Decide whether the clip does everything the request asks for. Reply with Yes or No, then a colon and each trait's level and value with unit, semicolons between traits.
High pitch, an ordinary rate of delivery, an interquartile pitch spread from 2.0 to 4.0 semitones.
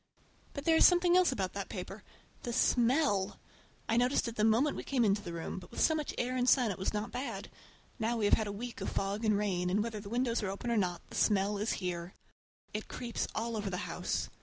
No: high, 215 Hz; fast, 240 wpm; average, 3.7 semitones